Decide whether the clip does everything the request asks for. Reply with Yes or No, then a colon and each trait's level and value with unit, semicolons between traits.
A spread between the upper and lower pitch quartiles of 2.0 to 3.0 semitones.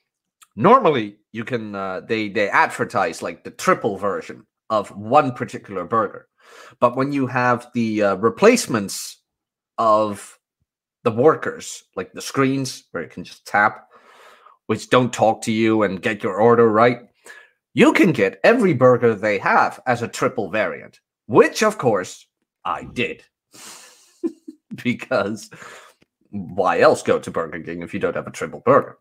No: average, 4.0 semitones